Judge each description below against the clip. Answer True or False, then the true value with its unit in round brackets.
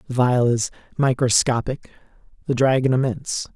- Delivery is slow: True (120 wpm)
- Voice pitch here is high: False (125 Hz)